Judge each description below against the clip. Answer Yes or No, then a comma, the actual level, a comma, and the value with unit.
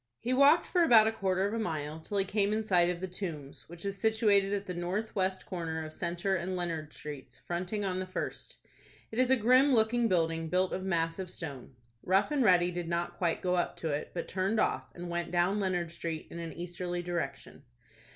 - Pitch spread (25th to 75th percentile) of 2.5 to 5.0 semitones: Yes, average, 3.0 semitones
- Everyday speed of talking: No, fast, 215 wpm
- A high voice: No, medium, 180 Hz